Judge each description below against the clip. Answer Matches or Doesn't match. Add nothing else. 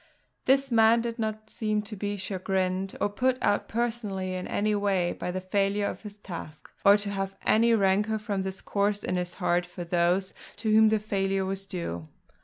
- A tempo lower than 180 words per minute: Doesn't match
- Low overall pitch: Doesn't match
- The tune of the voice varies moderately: Doesn't match